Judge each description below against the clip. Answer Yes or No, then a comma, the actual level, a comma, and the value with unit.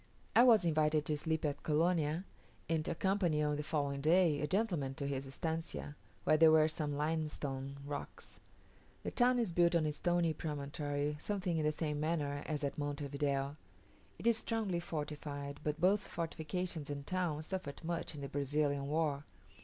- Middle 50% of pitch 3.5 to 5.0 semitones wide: No, average, 2.9 semitones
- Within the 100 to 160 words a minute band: No, average, 175 wpm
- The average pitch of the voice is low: No, medium, 155 Hz